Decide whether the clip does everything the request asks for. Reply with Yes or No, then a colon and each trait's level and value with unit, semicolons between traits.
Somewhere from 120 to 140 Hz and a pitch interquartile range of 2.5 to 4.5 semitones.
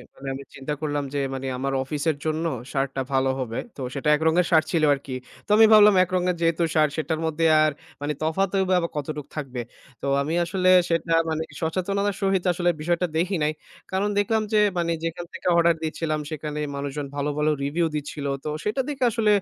No: medium, 160 Hz; average, 3.6 semitones